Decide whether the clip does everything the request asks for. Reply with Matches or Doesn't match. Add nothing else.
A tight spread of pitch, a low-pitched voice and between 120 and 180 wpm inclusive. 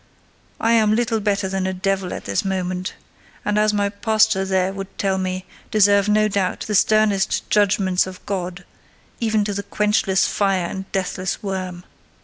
Doesn't match